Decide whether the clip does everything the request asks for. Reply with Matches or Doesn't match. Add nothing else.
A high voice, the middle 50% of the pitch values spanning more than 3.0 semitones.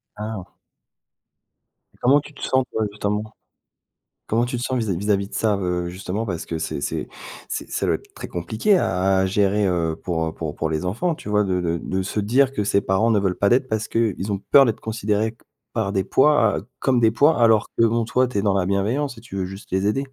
Doesn't match